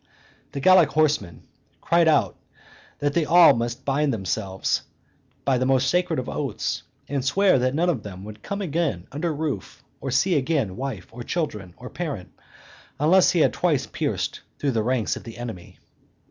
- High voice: No, low, 135 Hz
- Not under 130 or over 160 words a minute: No, average, 175 wpm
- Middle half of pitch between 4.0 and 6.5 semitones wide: Yes, wide, 5.6 semitones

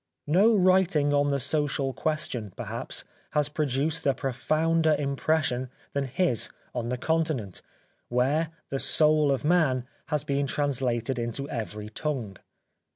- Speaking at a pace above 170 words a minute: No, average, 140 wpm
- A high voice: No, medium, 140 Hz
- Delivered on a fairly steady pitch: No, average, 3.5 semitones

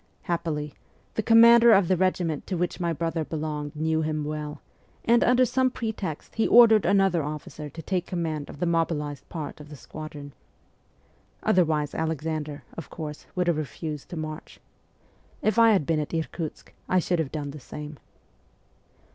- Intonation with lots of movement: No, average, 3.5 semitones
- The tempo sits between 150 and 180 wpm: Yes, average, 165 wpm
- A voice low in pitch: No, medium, 160 Hz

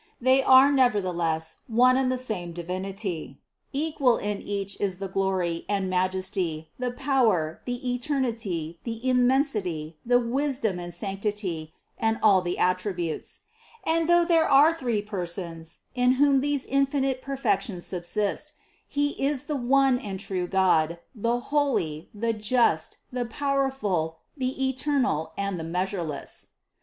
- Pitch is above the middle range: Yes, high, 215 Hz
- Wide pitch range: Yes, wide, 6.5 semitones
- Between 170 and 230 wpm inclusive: No, average, 140 wpm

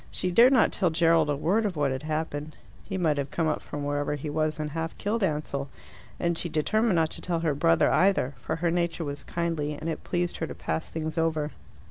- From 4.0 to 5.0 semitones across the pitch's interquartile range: No, average, 2.7 semitones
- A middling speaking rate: No, fast, 230 wpm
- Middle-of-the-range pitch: Yes, medium, 160 Hz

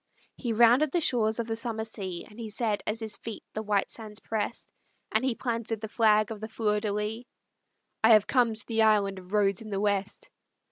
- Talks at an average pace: No, fast, 220 wpm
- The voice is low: No, high, 220 Hz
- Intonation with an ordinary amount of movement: No, narrow, 1.6 semitones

